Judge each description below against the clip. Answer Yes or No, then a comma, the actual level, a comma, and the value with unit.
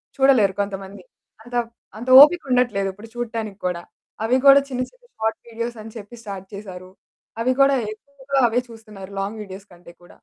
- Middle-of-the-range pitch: No, high, 220 Hz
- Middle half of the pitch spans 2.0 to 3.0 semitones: No, average, 4.1 semitones